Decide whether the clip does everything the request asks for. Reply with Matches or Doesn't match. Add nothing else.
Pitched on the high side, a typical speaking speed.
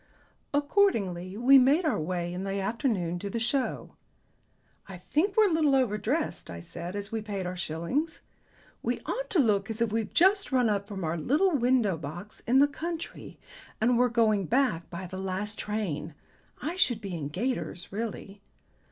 Matches